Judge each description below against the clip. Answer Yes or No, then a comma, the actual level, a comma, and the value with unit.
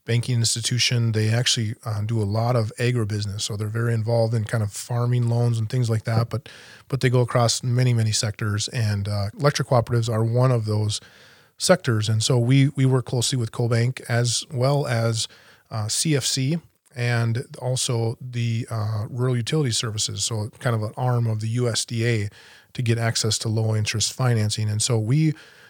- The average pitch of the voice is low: Yes, low, 115 Hz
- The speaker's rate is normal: Yes, average, 180 wpm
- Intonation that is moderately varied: No, narrow, 2.0 semitones